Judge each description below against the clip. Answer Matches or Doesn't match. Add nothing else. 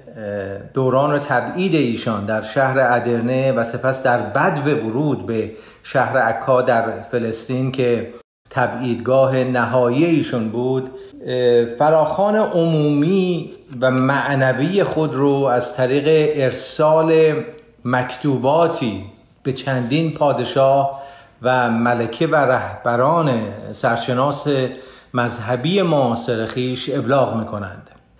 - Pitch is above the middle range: Doesn't match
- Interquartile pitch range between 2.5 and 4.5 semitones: Matches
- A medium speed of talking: Doesn't match